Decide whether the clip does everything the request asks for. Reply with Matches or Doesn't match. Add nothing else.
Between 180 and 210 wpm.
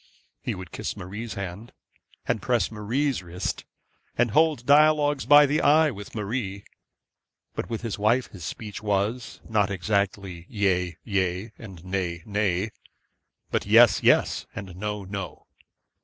Doesn't match